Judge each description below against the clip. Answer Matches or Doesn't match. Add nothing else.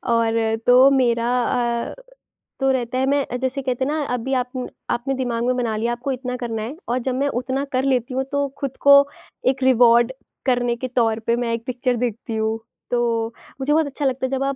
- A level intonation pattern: Matches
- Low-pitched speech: Doesn't match